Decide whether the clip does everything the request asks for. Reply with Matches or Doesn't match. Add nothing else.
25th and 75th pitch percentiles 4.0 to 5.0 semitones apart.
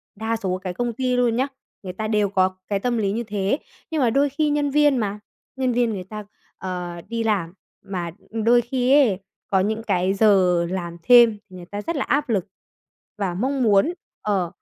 Matches